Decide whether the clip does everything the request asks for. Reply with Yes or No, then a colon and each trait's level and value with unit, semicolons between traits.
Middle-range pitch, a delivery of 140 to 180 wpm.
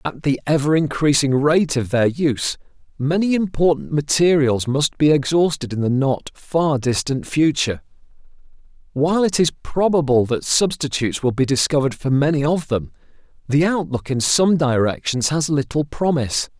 Yes: medium, 145 Hz; average, 150 wpm